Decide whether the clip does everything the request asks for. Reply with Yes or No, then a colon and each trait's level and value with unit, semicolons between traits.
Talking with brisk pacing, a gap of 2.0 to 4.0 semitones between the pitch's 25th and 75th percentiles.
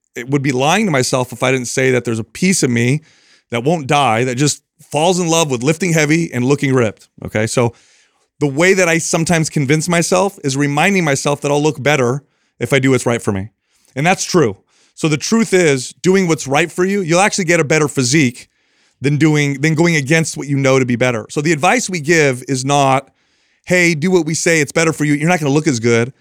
No: fast, 240 wpm; average, 4.4 semitones